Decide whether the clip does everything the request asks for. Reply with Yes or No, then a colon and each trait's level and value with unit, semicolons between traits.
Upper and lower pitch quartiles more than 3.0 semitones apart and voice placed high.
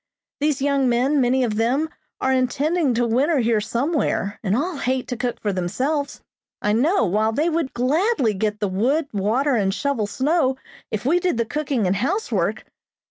Yes: average, 4.9 semitones; very high, 255 Hz